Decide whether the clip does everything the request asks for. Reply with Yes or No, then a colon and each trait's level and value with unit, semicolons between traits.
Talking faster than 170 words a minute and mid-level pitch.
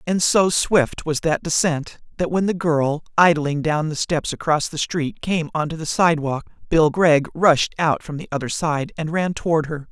Yes: average, 200 wpm; medium, 160 Hz